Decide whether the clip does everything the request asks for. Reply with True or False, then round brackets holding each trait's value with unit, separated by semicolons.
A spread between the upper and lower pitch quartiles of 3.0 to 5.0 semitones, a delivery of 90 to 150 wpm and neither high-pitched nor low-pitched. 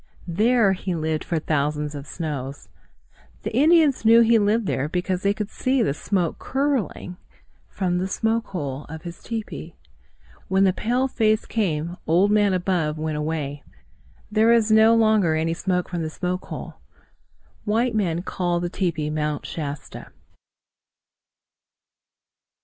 False (5.5 semitones; 145 wpm; 180 Hz)